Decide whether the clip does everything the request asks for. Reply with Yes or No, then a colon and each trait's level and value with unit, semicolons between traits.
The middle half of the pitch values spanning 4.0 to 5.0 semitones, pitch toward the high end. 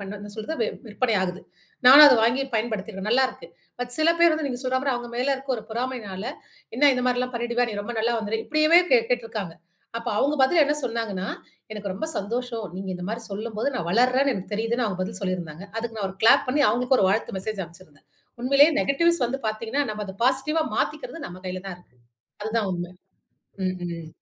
Yes: average, 4.7 semitones; high, 230 Hz